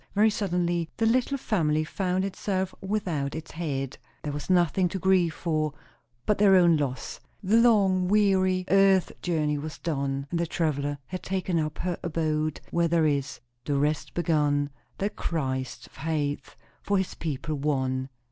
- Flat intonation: No, average, 4.2 semitones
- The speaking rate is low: No, average, 155 wpm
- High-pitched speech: No, medium, 165 Hz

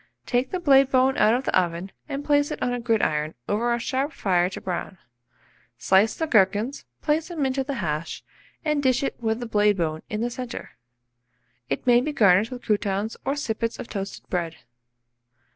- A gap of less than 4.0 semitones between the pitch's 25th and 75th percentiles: No, wide, 5.6 semitones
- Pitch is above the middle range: Yes, high, 230 Hz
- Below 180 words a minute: No, average, 190 wpm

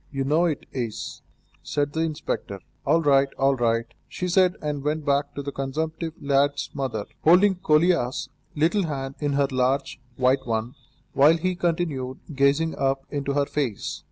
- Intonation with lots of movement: No, average, 3.1 semitones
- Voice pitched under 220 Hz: Yes, medium, 140 Hz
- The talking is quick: No, average, 160 wpm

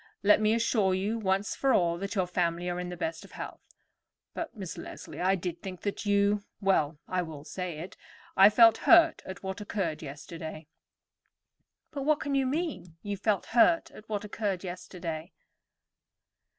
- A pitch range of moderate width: Yes, average, 3.5 semitones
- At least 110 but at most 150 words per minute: No, average, 170 wpm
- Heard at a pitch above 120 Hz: Yes, high, 190 Hz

